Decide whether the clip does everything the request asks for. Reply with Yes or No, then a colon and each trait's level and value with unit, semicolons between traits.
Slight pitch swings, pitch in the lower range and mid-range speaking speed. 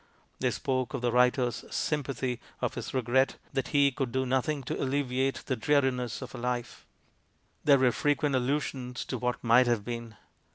Yes: narrow, 1.8 semitones; low, 130 Hz; average, 170 wpm